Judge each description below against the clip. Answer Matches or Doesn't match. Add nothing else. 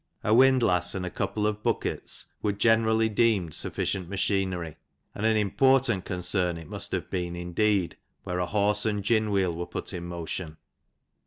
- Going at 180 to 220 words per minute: Doesn't match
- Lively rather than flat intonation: Doesn't match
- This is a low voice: Matches